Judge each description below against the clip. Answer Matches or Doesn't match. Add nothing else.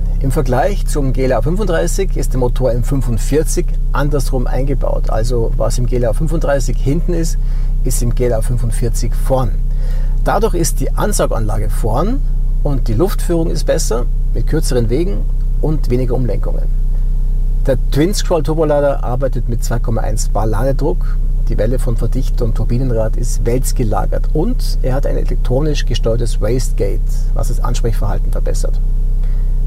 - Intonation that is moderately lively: Doesn't match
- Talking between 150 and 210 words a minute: Doesn't match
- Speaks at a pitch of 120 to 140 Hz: Matches